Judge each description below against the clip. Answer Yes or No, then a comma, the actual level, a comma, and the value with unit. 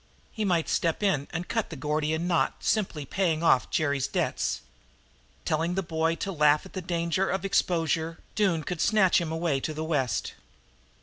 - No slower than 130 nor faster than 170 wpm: No, average, 180 wpm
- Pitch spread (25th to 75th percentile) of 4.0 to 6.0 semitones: No, average, 2.9 semitones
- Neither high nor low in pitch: Yes, medium, 165 Hz